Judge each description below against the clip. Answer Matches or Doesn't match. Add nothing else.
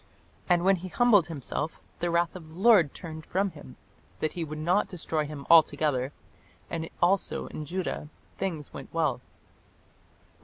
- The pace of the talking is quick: Doesn't match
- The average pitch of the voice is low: Doesn't match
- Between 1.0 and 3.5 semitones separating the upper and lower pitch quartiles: Matches